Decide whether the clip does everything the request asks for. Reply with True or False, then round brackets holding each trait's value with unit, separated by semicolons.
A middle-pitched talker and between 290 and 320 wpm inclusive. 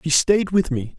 False (160 Hz; 245 wpm)